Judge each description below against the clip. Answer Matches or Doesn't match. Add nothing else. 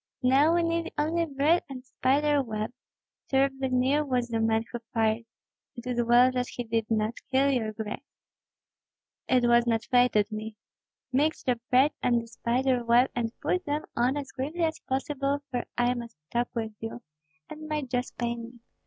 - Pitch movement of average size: Matches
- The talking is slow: Doesn't match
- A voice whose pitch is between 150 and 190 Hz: Doesn't match